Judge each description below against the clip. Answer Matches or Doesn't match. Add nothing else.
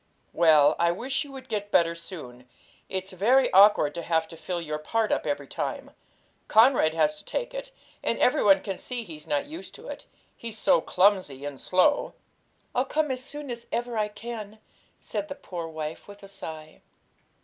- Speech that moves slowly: Doesn't match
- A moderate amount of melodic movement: Doesn't match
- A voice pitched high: Matches